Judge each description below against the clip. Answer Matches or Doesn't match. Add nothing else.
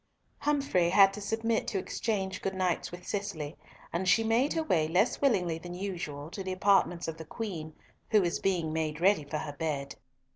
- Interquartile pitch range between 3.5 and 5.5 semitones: Matches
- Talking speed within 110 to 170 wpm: Doesn't match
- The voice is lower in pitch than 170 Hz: Doesn't match